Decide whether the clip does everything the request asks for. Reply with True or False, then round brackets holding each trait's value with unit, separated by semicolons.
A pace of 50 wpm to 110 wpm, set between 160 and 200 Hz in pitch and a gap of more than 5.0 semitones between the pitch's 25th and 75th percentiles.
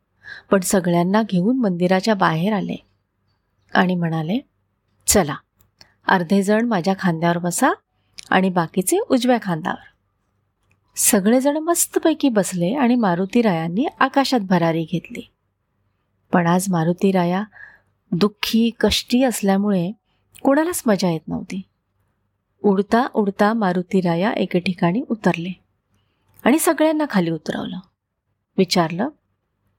True (100 wpm; 190 Hz; 5.4 semitones)